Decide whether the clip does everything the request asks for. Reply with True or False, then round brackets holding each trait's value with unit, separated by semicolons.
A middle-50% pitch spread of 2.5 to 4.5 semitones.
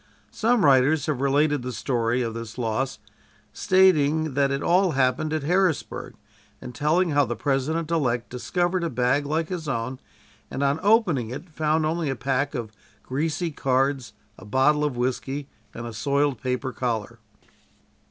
True (3.8 semitones)